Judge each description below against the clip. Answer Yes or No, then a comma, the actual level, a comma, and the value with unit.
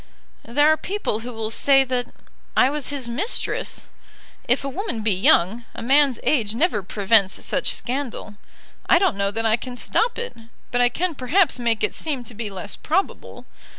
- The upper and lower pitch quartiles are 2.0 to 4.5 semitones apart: No, average, 5.0 semitones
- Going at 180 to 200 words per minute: Yes, average, 185 wpm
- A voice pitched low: No, high, 245 Hz